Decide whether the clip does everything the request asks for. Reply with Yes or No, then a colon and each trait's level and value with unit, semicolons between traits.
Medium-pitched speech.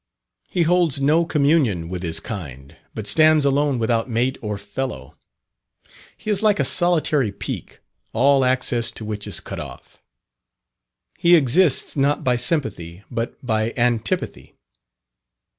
No: low, 125 Hz